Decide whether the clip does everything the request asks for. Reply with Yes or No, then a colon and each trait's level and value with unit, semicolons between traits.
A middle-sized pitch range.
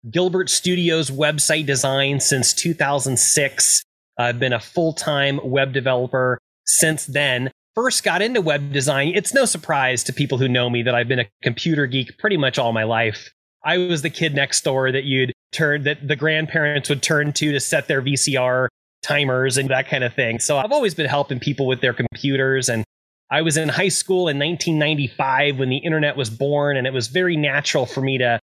Yes: average, 3.2 semitones